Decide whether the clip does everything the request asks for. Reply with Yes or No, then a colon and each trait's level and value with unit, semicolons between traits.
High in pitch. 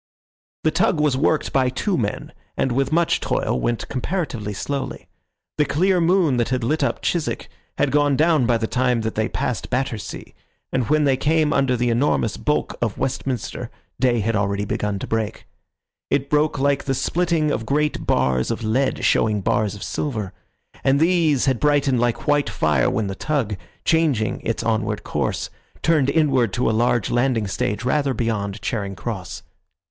No: low, 125 Hz